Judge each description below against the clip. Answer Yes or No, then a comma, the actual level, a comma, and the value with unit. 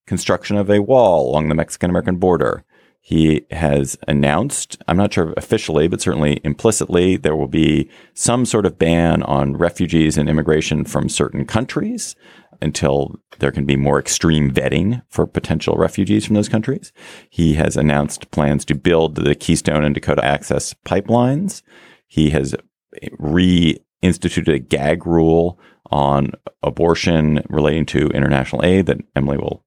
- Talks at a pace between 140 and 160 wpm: Yes, average, 150 wpm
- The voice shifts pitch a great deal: No, average, 3.8 semitones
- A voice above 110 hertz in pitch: No, very low, 80 Hz